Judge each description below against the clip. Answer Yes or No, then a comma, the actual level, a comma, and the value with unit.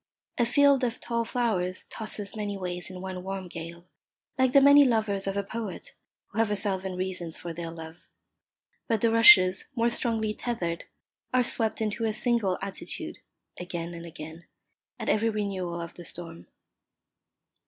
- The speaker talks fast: No, average, 165 wpm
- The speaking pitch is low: No, high, 200 Hz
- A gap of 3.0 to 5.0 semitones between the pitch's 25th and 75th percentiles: Yes, average, 4.4 semitones